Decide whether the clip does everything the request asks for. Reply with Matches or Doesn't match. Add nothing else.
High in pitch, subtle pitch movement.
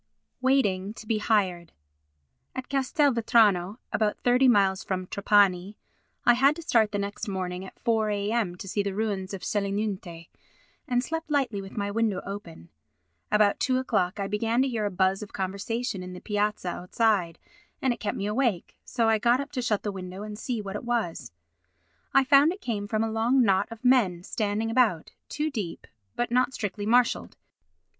Doesn't match